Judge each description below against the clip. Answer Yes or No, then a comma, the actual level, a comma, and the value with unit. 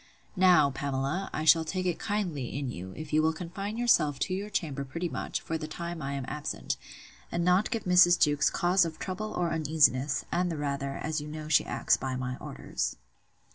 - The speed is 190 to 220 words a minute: Yes, fast, 205 wpm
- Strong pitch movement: No, average, 4.1 semitones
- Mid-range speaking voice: Yes, medium, 155 Hz